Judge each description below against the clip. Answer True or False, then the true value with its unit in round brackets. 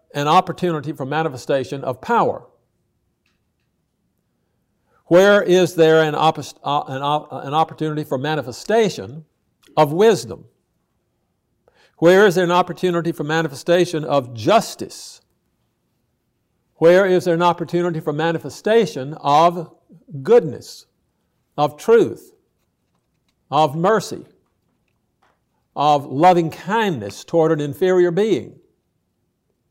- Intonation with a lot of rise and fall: False (3.3 semitones)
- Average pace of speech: False (95 wpm)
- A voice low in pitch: False (160 Hz)